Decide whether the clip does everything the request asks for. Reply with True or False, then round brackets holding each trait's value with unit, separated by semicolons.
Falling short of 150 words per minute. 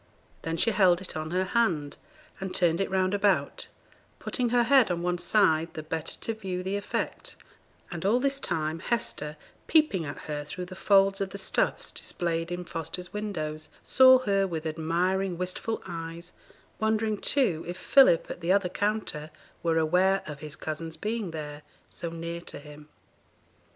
False (170 wpm)